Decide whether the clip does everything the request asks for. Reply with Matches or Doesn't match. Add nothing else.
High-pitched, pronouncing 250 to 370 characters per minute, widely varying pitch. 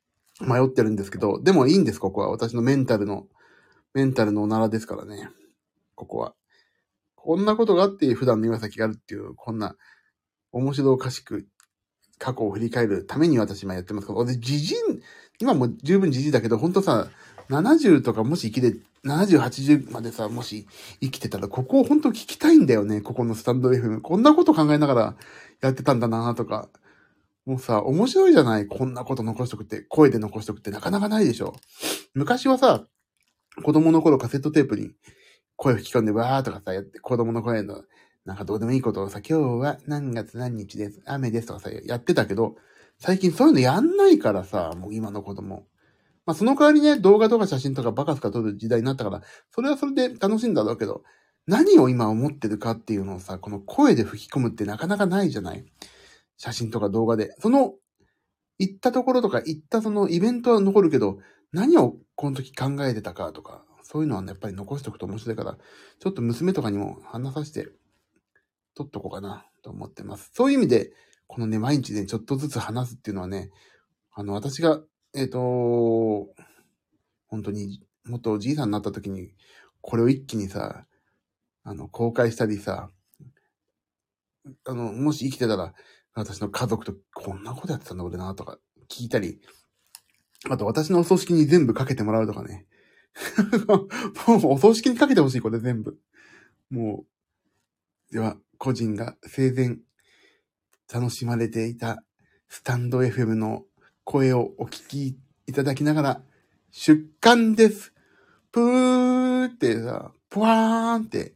Doesn't match